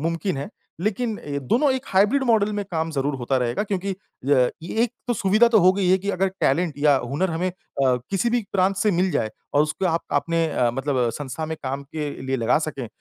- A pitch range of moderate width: No, wide, 5.9 semitones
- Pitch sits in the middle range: Yes, medium, 165 Hz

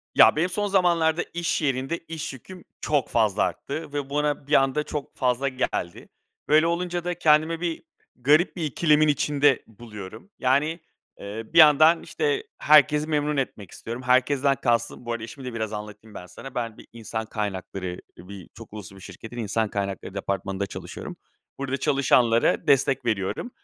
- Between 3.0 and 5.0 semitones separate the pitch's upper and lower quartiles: No, wide, 5.5 semitones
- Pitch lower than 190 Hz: Yes, low, 135 Hz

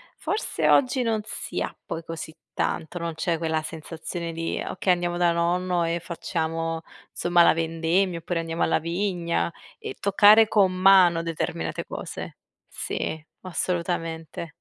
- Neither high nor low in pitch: Yes, medium, 170 Hz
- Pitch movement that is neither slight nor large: No, narrow, 1.9 semitones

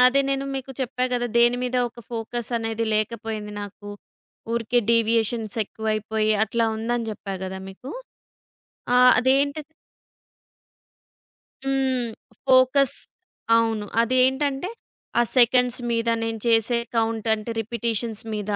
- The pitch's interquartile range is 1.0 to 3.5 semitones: Yes, narrow, 2.4 semitones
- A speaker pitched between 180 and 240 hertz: Yes, high, 230 Hz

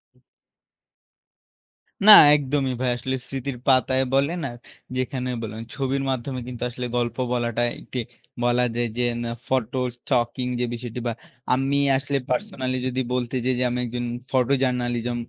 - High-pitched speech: No, low, 125 Hz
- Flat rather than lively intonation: Yes, narrow, 1.5 semitones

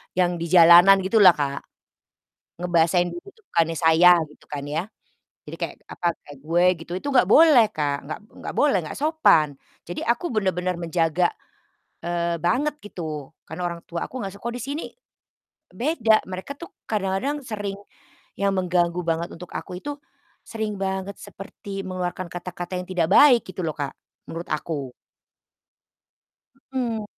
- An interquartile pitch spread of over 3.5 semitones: Yes, average, 4.0 semitones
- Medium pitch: Yes, medium, 180 Hz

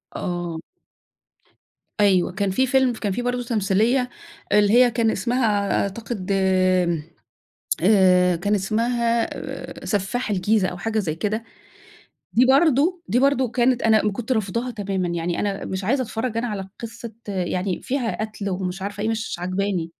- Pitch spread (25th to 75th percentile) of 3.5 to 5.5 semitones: Yes, average, 4.0 semitones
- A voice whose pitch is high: Yes, high, 210 Hz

